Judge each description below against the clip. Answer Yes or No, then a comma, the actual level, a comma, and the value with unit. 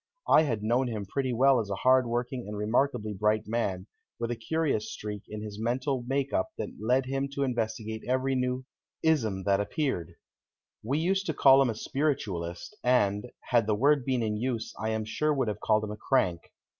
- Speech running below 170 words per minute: No, average, 200 wpm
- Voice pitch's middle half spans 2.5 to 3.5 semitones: No, average, 4.0 semitones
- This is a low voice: Yes, low, 120 Hz